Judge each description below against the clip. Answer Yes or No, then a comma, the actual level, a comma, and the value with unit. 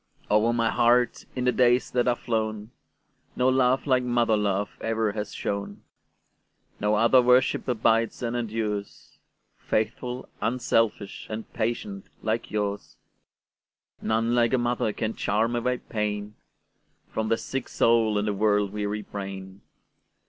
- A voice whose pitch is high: No, low, 110 Hz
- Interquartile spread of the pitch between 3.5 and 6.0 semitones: No, narrow, 2.5 semitones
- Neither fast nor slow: No, slow, 120 wpm